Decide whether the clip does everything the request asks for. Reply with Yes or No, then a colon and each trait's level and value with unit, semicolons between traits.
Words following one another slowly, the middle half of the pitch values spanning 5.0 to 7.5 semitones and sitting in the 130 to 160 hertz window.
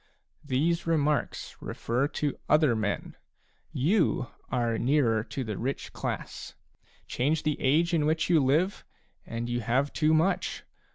No: slow, 130 wpm; average, 4.6 semitones; medium, 140 Hz